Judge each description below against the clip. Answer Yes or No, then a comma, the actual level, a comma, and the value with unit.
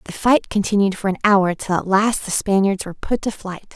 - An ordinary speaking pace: No, fast, 240 wpm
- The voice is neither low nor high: No, high, 200 Hz